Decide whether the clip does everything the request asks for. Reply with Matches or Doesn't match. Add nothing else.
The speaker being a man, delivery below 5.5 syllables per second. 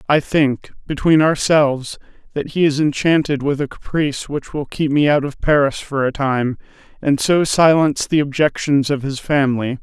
Matches